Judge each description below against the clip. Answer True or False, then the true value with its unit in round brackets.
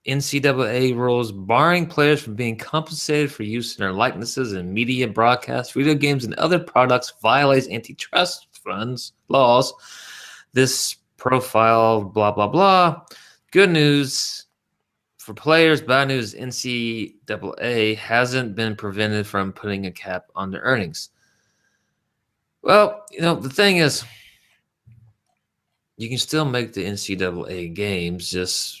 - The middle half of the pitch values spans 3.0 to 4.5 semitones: False (5.1 semitones)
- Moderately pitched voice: False (125 Hz)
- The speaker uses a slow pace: True (125 wpm)